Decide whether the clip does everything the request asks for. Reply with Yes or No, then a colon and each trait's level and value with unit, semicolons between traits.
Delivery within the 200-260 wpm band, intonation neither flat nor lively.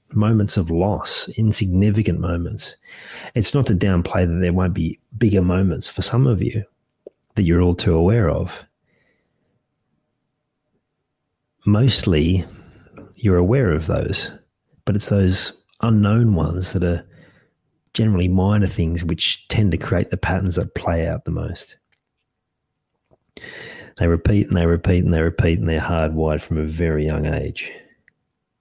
No: average, 140 wpm; average, 3.7 semitones